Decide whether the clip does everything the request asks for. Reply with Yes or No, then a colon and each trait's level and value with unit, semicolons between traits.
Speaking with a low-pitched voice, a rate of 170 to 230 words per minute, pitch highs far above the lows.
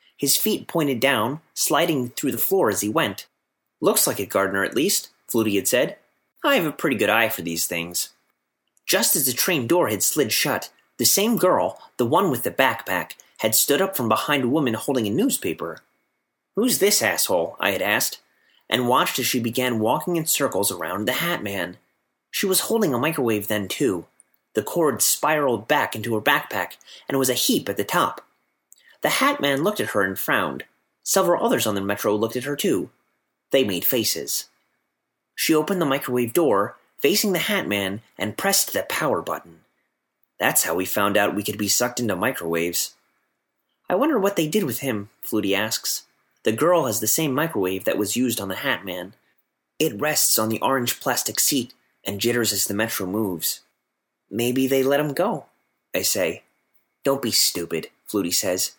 Yes: low, 120 Hz; average, 190 wpm; wide, 5.9 semitones